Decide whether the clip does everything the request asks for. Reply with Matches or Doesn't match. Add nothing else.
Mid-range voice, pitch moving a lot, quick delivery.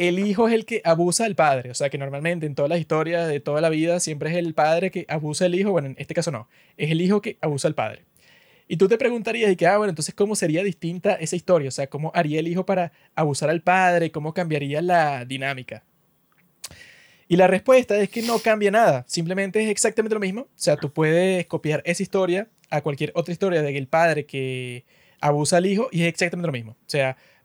Doesn't match